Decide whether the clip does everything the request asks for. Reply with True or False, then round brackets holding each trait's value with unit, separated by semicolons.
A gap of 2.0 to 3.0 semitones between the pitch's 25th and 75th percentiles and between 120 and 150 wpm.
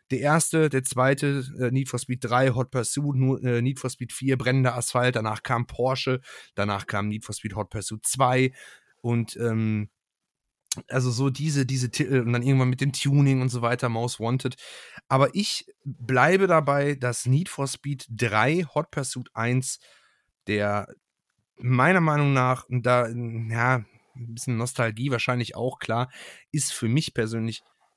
False (2.5 semitones; 160 wpm)